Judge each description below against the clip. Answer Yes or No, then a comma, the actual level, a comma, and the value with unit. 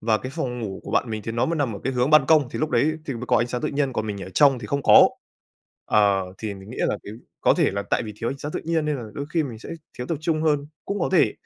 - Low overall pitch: Yes, low, 125 Hz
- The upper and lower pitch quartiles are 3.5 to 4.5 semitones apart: No, average, 5.2 semitones